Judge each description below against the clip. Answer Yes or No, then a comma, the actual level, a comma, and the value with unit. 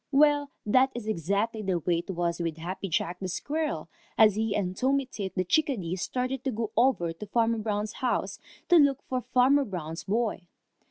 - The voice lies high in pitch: Yes, high, 215 Hz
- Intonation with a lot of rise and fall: Yes, wide, 6.0 semitones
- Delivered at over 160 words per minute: Yes, average, 180 wpm